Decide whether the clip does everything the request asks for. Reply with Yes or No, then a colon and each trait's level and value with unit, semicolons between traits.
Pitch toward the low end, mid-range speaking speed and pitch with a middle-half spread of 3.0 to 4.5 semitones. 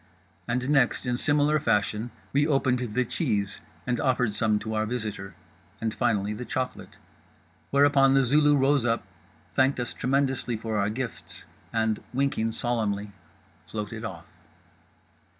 No: low, 120 Hz; slow, 130 wpm; average, 3.9 semitones